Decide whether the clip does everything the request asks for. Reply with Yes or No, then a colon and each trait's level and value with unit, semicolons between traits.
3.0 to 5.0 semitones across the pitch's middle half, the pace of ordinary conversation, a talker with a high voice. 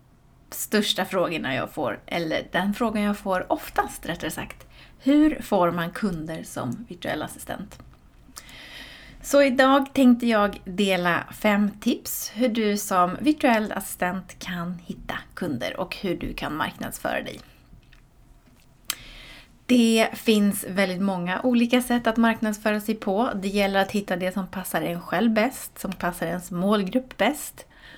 Yes: average, 4.1 semitones; average, 140 wpm; high, 205 Hz